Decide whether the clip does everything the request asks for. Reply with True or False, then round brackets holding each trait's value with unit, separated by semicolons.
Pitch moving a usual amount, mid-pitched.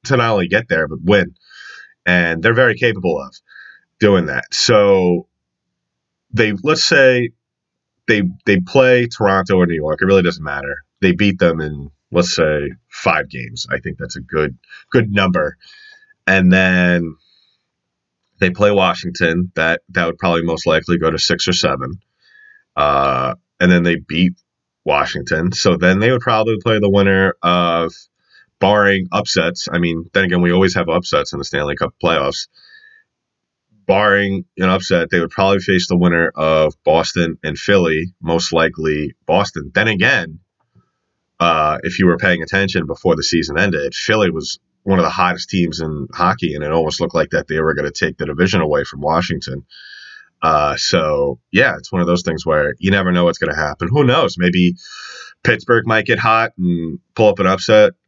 False (3.2 semitones; 90 Hz)